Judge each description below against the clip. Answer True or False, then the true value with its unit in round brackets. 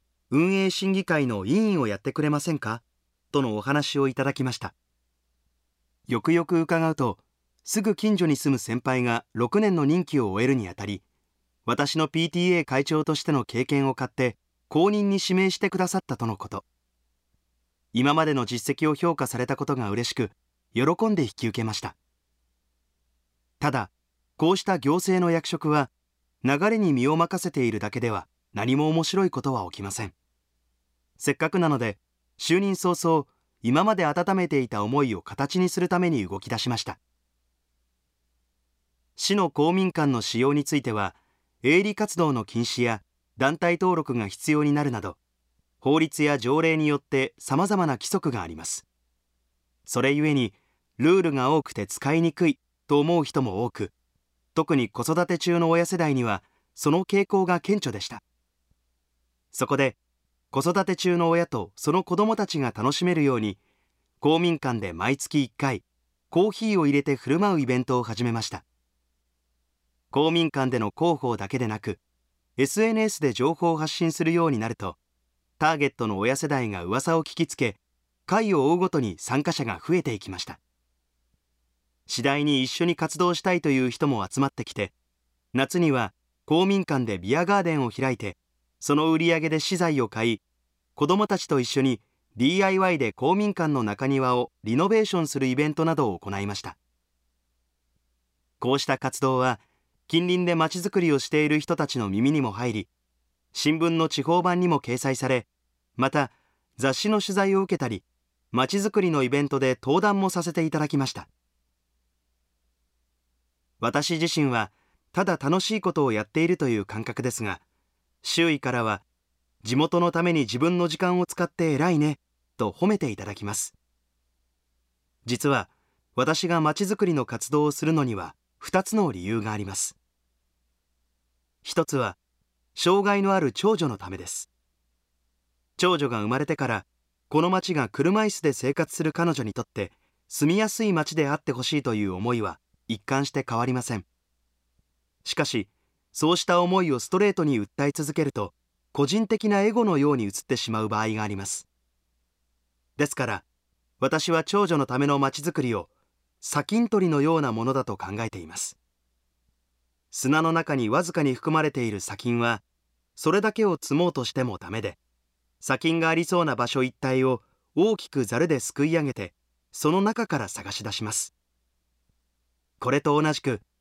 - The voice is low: True (130 Hz)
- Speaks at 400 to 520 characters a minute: False (305 characters per minute)